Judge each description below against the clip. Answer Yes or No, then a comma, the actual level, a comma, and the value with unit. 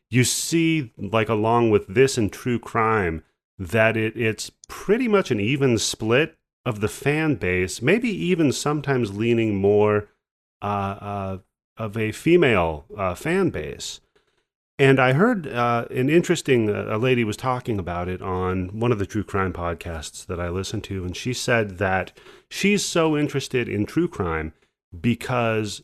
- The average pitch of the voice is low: Yes, low, 110 Hz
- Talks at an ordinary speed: Yes, average, 160 wpm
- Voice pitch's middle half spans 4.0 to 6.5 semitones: Yes, average, 4.8 semitones